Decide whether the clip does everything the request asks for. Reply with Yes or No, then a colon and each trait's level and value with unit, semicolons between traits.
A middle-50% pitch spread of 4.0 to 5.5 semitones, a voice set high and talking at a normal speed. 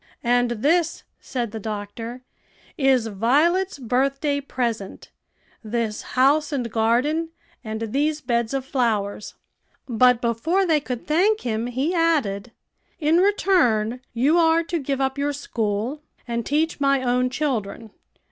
No: average, 4.7 semitones; very high, 255 Hz; slow, 130 wpm